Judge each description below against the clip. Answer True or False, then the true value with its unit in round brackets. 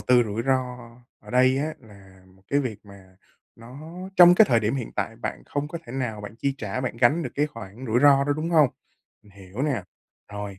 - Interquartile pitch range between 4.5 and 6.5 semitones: True (5.1 semitones)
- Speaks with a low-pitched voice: True (125 Hz)